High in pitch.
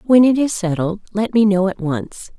Yes: high, 200 Hz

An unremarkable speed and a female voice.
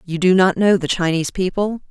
No: fast, 220 wpm; female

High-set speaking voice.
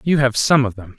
No: low, 125 Hz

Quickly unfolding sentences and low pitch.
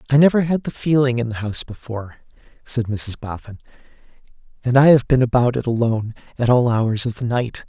No: average, 195 wpm; low, 120 Hz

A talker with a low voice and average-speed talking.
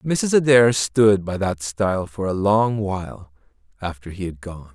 Yes: low, 100 Hz; average, 175 wpm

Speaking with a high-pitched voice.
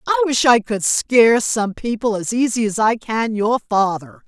Yes: high, 225 Hz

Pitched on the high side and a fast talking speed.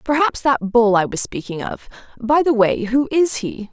Yes: high, 245 Hz; fast, 210 wpm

